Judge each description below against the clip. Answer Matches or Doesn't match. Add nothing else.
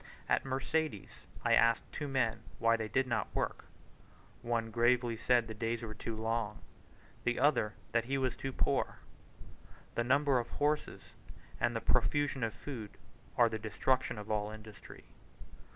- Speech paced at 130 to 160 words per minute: Matches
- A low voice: Matches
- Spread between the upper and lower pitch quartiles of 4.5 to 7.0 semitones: Doesn't match